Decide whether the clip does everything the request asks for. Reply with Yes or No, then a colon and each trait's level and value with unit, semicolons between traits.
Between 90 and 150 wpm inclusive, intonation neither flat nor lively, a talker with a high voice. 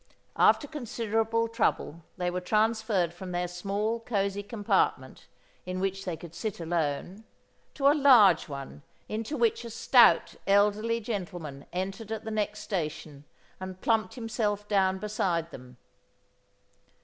Yes: slow, 135 wpm; average, 4.0 semitones; high, 200 Hz